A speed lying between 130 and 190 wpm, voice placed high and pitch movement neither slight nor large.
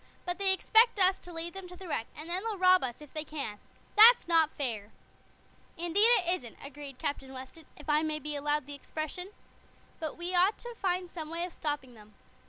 No: fast, 205 wpm; very high, 325 Hz; average, 4.1 semitones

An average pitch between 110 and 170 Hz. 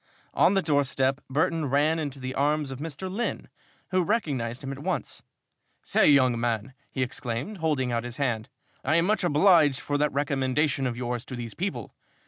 Yes: medium, 140 Hz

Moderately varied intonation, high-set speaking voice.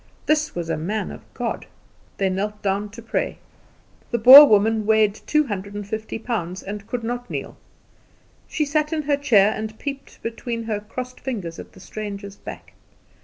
Yes: average, 3.7 semitones; high, 220 Hz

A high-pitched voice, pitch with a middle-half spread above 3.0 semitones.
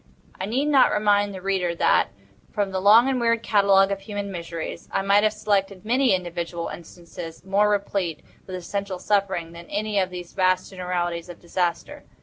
No: high, 195 Hz; average, 2.7 semitones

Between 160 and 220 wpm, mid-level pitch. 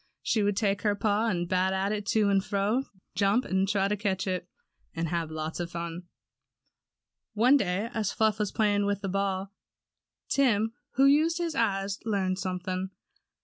No: average, 170 wpm; high, 200 Hz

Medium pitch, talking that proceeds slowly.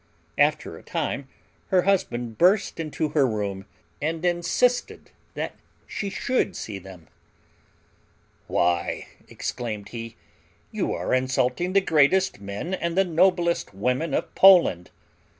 Yes: medium, 155 Hz; slow, 120 wpm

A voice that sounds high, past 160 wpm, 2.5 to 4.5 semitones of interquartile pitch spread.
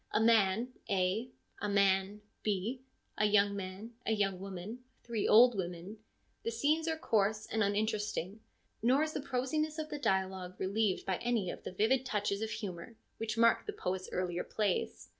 Yes: high, 210 Hz; average, 170 wpm; average, 3.5 semitones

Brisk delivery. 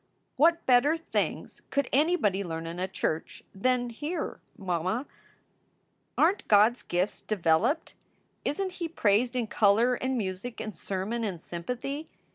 No: average, 145 wpm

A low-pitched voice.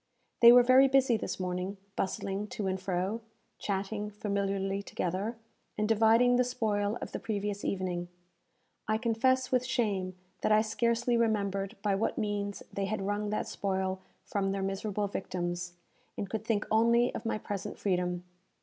No: high, 205 Hz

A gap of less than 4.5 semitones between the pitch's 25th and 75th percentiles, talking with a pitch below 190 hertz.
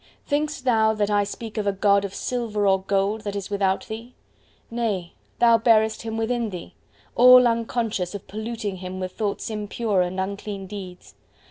No: average, 2.7 semitones; high, 210 Hz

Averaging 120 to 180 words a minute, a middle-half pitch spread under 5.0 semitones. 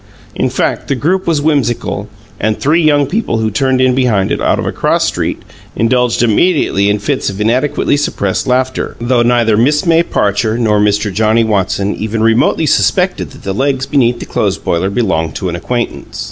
No: average, 190 wpm; average, 4.2 semitones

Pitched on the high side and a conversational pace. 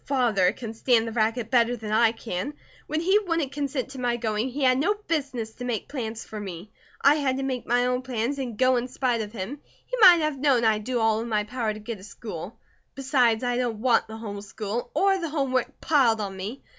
No: high, 245 Hz; fast, 235 wpm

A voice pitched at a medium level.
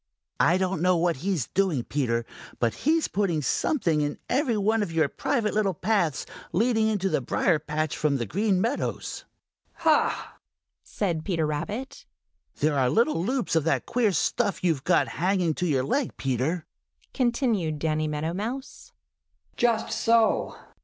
Yes: medium, 180 Hz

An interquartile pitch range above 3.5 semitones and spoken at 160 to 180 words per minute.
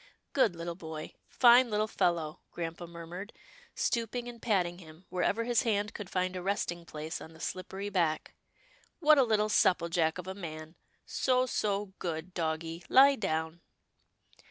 Yes: average, 4.4 semitones; average, 170 wpm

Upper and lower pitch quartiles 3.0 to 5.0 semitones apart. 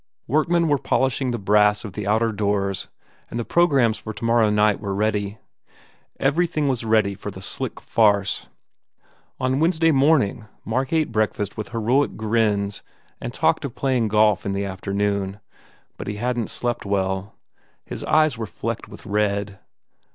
Yes: average, 4.0 semitones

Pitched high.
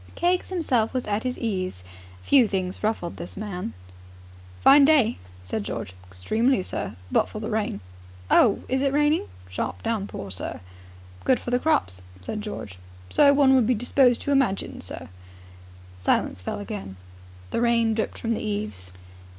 Yes: high, 220 Hz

